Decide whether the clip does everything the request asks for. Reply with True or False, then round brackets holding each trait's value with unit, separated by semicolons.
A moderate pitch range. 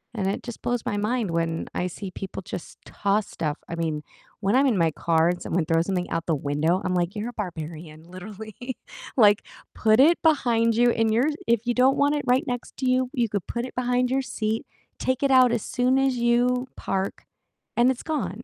False (5.9 semitones)